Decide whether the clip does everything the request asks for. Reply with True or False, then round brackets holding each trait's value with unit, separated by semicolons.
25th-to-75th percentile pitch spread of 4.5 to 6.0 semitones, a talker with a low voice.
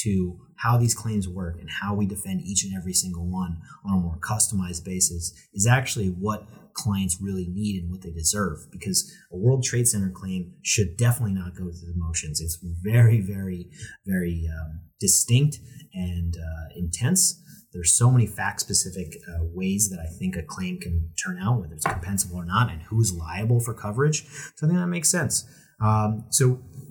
True (4.8 semitones; 95 Hz)